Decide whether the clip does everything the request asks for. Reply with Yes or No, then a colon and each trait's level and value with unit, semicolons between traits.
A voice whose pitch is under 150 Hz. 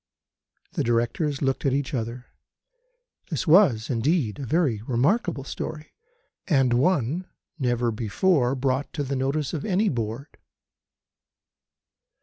Yes: low, 135 Hz